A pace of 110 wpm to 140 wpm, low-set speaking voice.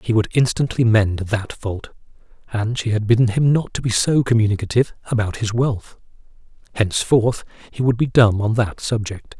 No: average, 170 wpm; low, 110 Hz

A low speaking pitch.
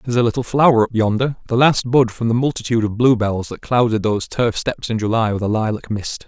Yes: low, 115 Hz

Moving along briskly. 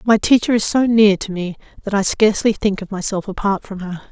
Yes: fast, 235 wpm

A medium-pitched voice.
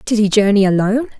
No: high, 210 Hz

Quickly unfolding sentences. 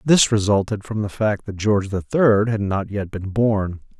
Yes: fast, 210 wpm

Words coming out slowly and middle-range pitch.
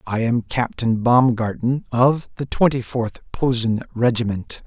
No: slow, 130 wpm; low, 120 Hz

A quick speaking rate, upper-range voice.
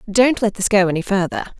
Yes: fast, 225 wpm; high, 195 Hz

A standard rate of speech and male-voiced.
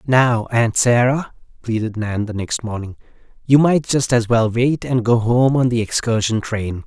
Yes: average, 185 wpm; male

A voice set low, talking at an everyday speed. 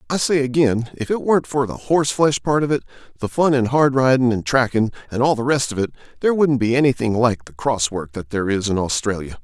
No: low, 125 Hz; fast, 250 wpm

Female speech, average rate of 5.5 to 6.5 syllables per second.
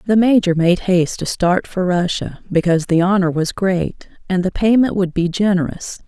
No: female; 5.0 syllables/s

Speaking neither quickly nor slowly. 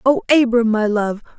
Yes: average, 175 wpm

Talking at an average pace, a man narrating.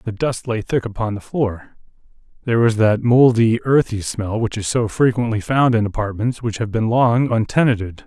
Yes: average, 180 wpm; male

